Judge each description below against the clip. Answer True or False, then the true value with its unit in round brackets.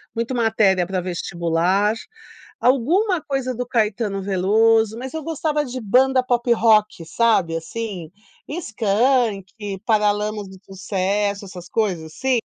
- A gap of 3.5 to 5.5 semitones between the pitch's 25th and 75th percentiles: True (4.4 semitones)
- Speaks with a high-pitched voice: True (215 Hz)